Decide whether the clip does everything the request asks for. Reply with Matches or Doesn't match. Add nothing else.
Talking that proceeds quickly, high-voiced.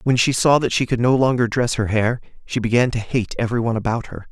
Doesn't match